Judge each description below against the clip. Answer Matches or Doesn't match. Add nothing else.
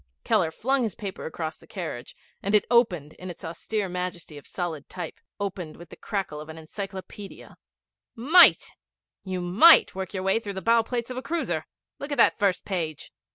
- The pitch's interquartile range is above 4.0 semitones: Matches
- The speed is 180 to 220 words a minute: Matches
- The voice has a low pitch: Doesn't match